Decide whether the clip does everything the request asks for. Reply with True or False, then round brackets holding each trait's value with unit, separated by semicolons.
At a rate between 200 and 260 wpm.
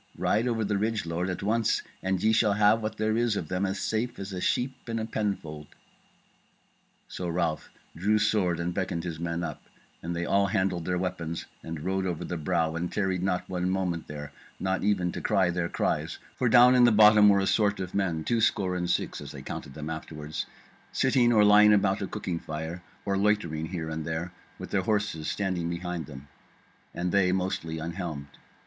True (205 wpm)